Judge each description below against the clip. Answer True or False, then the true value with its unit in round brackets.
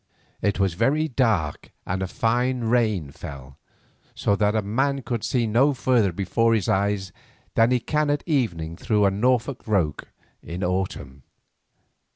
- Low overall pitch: True (110 Hz)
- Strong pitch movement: False (4.7 semitones)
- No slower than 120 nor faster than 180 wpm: True (155 wpm)